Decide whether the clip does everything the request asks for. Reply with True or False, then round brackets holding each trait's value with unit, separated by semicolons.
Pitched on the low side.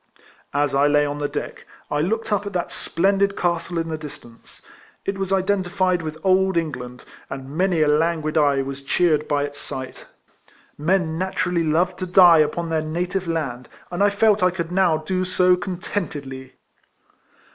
False (170 Hz)